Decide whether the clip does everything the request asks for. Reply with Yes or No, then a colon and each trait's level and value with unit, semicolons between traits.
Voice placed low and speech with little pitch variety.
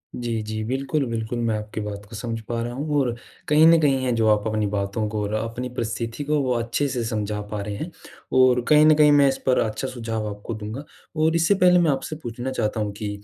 No: low, 120 Hz; average, 4.3 semitones